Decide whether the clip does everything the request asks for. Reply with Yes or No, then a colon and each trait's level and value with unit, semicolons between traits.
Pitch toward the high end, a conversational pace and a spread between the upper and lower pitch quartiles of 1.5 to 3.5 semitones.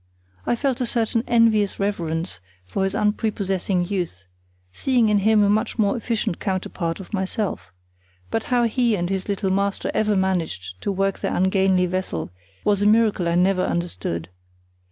Yes: high, 195 Hz; average, 160 wpm; average, 3.2 semitones